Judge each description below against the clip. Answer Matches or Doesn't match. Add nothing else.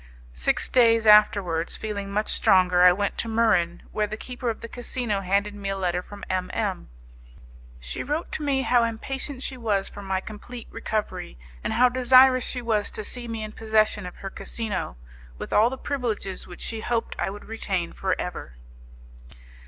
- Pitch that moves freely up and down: Doesn't match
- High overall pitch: Matches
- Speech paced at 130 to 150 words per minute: Doesn't match